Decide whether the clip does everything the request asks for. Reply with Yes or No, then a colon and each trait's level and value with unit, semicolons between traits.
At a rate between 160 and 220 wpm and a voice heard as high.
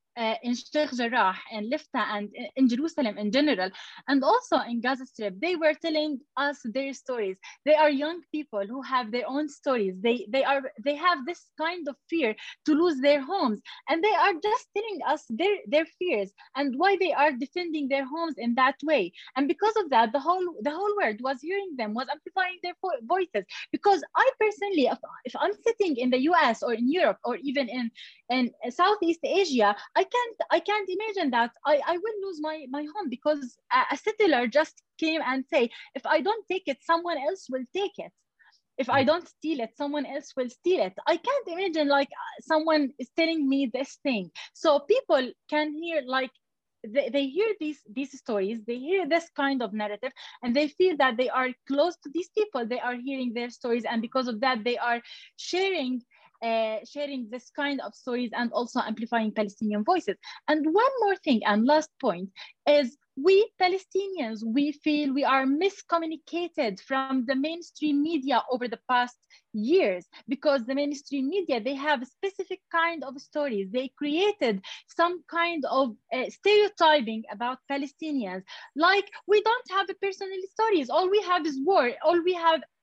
Yes: average, 185 wpm; very high, 290 Hz